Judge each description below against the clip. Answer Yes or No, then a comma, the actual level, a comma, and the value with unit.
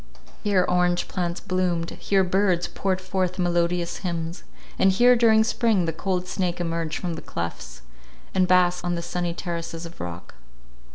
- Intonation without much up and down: Yes, narrow, 1.7 semitones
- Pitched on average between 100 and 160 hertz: No, medium, 180 Hz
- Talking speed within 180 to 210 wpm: No, average, 160 wpm